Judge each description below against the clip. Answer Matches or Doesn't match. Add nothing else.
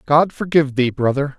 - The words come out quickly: Doesn't match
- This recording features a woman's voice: Doesn't match